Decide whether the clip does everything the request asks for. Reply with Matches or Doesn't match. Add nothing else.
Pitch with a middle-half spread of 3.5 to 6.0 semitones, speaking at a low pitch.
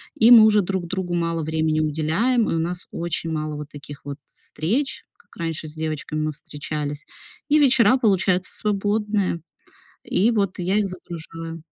Doesn't match